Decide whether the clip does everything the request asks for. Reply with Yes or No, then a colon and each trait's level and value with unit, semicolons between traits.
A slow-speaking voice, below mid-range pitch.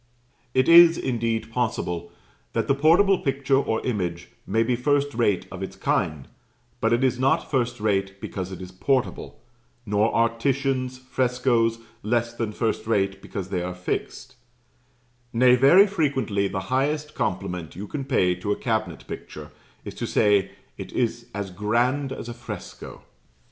No: average, 160 wpm; low, 115 Hz